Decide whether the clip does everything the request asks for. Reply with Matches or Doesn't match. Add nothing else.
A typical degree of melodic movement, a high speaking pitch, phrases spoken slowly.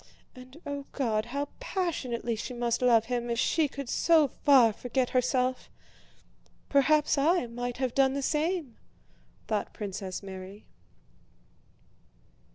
Matches